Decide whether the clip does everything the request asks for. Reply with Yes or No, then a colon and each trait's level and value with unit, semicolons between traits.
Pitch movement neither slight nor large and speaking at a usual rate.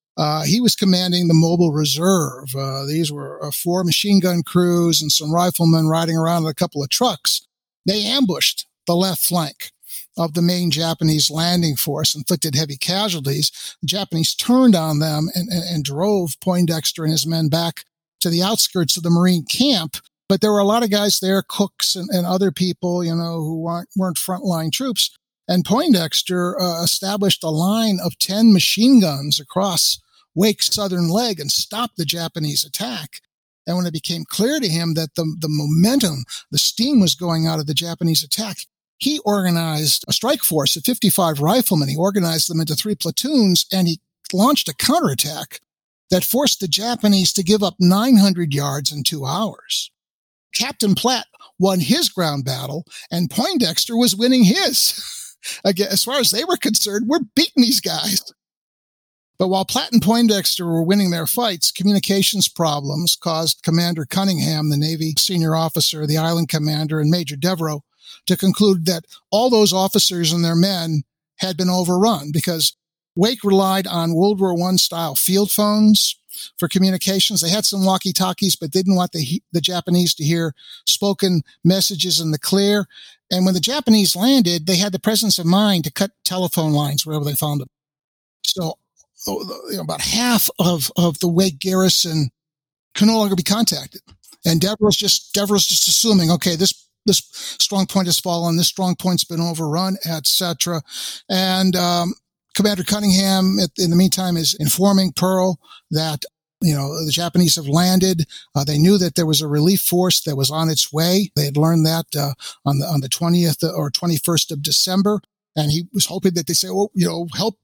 Yes: average, 3.4 semitones; average, 180 wpm